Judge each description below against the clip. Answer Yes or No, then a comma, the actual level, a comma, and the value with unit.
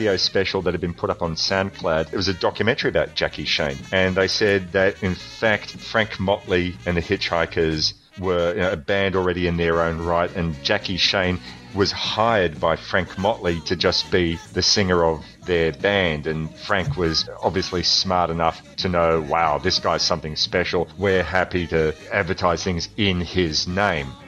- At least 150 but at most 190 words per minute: Yes, average, 180 wpm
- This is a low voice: Yes, very low, 90 Hz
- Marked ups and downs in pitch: No, narrow, 2.5 semitones